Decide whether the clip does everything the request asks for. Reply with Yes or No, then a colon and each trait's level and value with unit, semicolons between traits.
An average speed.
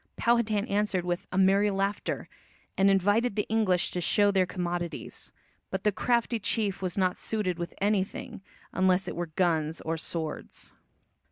Yes: average, 155 wpm